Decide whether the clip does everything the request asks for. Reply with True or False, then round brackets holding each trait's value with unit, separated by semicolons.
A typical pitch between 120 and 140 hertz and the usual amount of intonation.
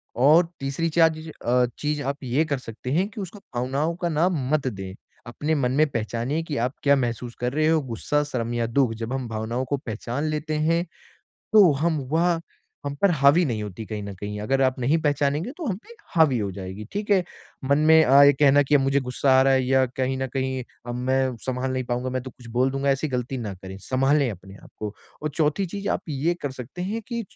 True (135 Hz; 3.9 semitones)